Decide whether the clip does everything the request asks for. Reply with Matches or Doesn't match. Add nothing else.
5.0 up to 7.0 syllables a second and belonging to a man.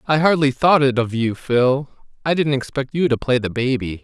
Matches